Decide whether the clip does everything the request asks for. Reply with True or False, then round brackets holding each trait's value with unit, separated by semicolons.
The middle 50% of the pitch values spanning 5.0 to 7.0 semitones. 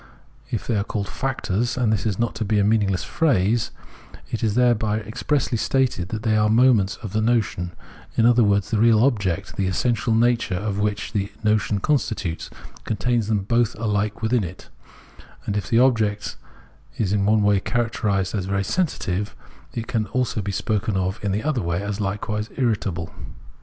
False (2.8 semitones)